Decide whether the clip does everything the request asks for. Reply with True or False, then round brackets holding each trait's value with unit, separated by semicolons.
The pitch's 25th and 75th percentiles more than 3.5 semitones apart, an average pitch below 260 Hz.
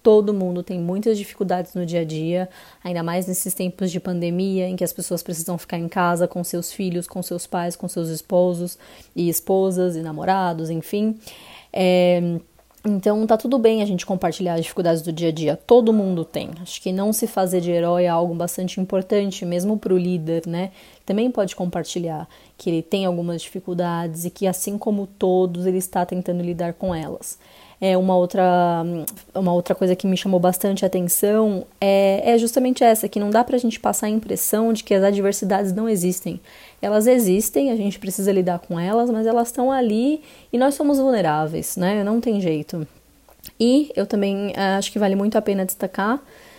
False (2.9 semitones; 185 Hz)